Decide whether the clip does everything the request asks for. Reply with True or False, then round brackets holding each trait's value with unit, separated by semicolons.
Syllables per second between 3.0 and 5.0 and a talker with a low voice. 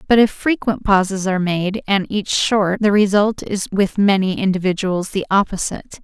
False (4.9 syllables/s; 195 Hz)